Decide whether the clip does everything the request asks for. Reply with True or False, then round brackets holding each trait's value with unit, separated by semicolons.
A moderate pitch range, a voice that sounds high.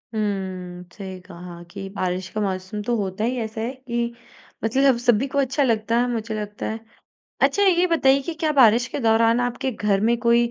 True (4.0 semitones; 225 Hz)